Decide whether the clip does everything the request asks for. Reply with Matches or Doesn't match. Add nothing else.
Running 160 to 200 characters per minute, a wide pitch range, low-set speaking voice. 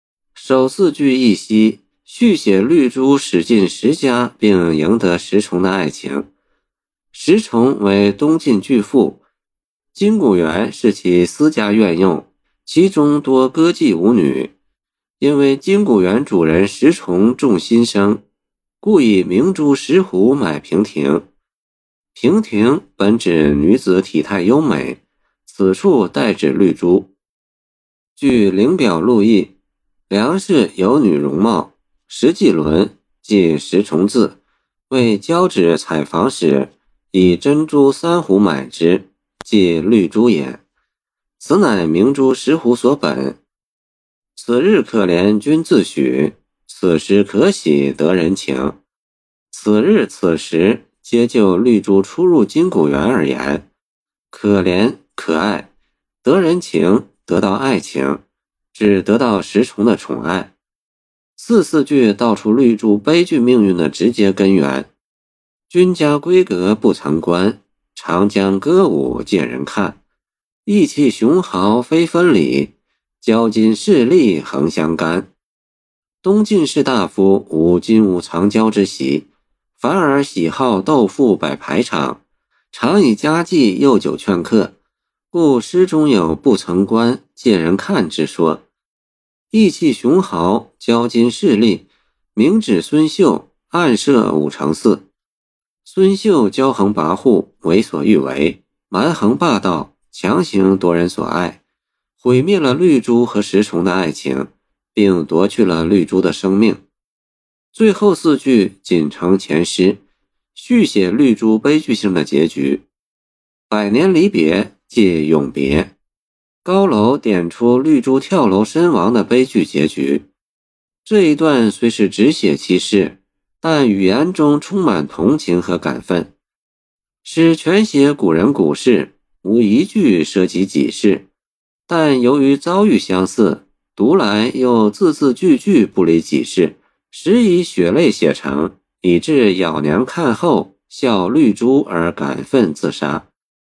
Matches